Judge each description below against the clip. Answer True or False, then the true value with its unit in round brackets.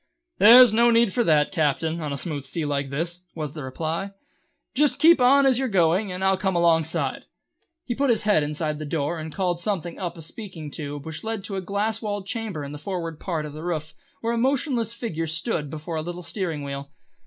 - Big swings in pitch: True (5.7 semitones)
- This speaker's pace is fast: True (220 wpm)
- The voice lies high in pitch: False (175 Hz)